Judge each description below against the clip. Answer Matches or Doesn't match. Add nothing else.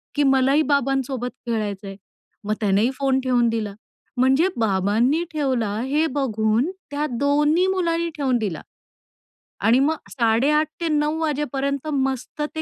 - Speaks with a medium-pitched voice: Doesn't match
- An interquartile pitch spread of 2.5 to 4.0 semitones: Doesn't match